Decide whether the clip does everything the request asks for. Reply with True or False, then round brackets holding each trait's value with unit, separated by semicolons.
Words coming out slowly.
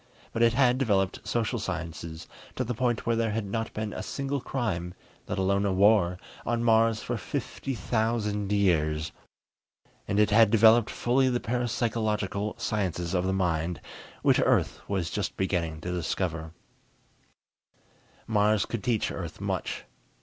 False (150 wpm)